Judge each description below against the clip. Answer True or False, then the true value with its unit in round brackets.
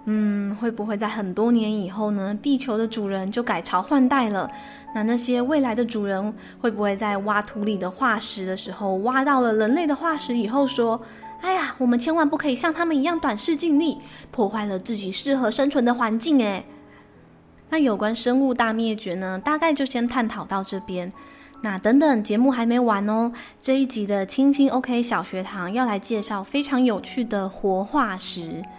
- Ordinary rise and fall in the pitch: True (4.7 semitones)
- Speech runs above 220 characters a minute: True (280 characters per minute)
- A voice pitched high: True (230 Hz)